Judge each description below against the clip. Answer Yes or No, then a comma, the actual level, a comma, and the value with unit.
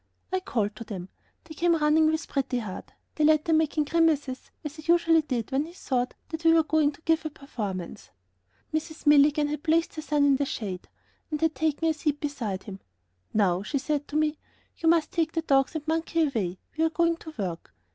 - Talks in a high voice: Yes, very high, 300 Hz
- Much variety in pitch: No, average, 3.3 semitones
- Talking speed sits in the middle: No, fast, 215 wpm